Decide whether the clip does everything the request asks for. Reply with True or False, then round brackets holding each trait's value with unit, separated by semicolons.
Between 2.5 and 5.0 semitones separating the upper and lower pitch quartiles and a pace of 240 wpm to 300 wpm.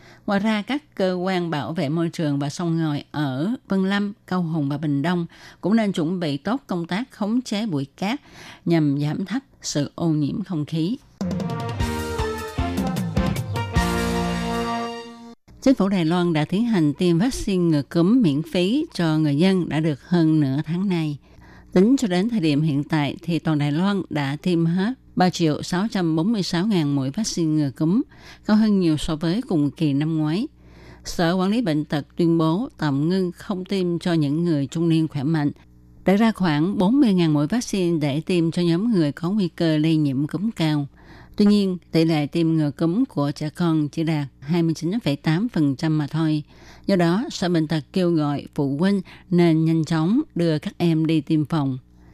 False (4.1 semitones; 185 wpm)